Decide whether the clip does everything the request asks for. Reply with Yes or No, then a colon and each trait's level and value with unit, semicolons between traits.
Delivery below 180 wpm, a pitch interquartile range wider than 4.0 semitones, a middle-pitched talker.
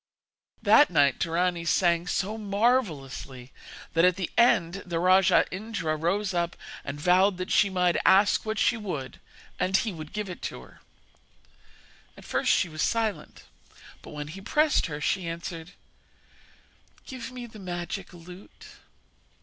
No: average, 150 wpm; average, 3.5 semitones; medium, 180 Hz